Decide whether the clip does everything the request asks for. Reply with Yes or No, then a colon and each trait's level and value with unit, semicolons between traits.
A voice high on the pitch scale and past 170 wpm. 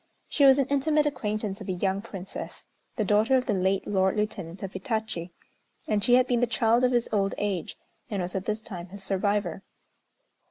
Yes: high, 210 Hz; average, 200 wpm